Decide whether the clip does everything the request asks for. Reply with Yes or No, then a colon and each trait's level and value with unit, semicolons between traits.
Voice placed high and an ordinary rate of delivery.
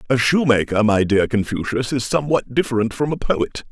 No: low, 125 Hz; average, 180 wpm